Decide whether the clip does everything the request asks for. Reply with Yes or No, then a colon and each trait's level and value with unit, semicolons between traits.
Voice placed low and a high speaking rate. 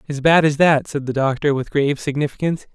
No: medium, 145 Hz; fast, 220 wpm